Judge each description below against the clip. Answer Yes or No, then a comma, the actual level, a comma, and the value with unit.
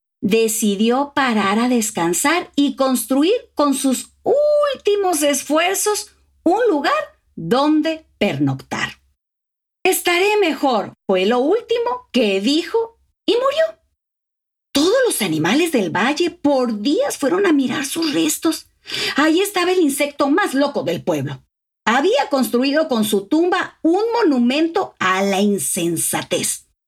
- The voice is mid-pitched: No, very high, 290 Hz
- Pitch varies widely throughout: Yes, wide, 6.4 semitones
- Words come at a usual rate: No, slow, 120 wpm